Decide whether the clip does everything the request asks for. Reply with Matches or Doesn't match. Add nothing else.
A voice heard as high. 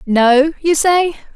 Matches